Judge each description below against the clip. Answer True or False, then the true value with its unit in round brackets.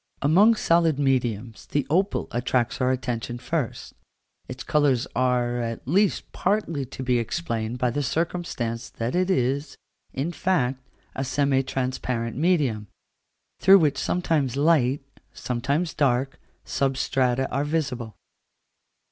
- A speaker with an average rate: False (120 wpm)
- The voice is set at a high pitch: False (135 Hz)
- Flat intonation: False (4.2 semitones)